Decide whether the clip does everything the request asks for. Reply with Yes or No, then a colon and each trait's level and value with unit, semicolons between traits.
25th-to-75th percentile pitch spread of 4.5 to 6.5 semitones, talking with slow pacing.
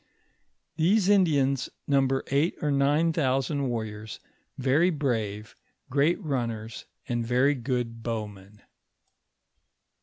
No: average, 4.1 semitones; slow, 110 wpm